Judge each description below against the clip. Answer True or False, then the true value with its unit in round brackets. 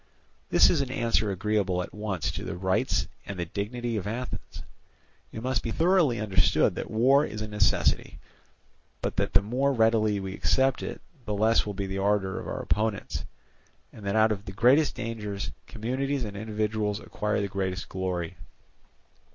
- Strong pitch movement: False (3.0 semitones)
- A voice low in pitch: True (105 Hz)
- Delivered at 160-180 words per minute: True (175 wpm)